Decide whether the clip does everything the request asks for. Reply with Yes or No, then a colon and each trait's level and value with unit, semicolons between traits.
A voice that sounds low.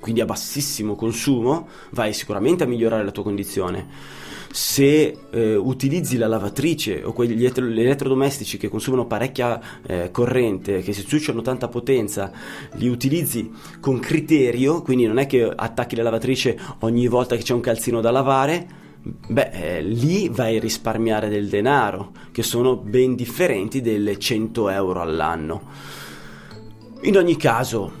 Yes: low, 120 Hz